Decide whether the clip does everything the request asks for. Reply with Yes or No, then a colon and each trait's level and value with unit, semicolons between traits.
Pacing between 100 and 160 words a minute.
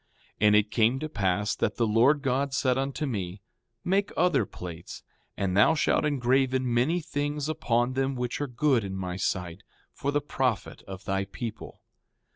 No: average, 175 wpm